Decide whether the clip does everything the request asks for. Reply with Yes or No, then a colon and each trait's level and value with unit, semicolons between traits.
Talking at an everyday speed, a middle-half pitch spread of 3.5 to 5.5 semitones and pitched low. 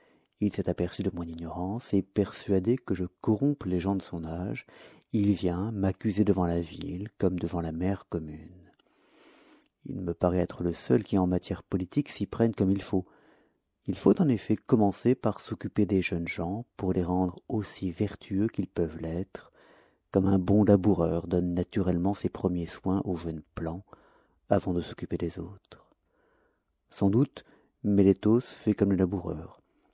No: average, 170 wpm; average, 2.7 semitones; very low, 95 Hz